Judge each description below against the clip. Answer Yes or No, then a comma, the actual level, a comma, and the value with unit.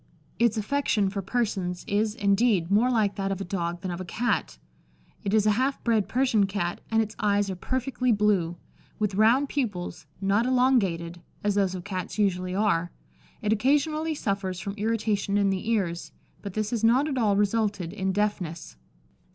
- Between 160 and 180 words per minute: Yes, average, 175 wpm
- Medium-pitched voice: No, high, 205 Hz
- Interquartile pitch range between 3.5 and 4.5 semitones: No, average, 3.1 semitones